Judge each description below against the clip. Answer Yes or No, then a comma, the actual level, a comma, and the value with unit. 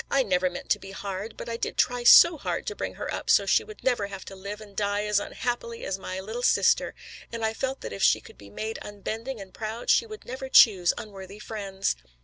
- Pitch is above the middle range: Yes, high, 210 Hz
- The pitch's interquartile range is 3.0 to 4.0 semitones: Yes, average, 3.7 semitones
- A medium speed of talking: No, fast, 240 wpm